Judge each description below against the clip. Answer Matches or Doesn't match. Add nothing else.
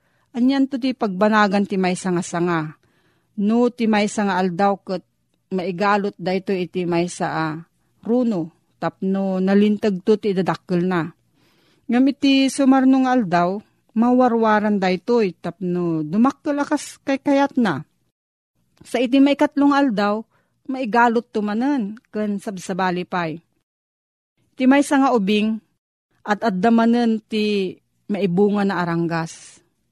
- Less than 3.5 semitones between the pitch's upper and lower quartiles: Doesn't match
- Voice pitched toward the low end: Doesn't match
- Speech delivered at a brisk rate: Doesn't match